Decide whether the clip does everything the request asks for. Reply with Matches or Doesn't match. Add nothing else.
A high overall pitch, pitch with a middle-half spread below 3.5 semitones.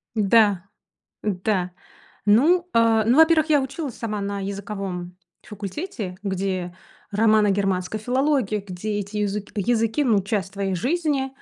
Doesn't match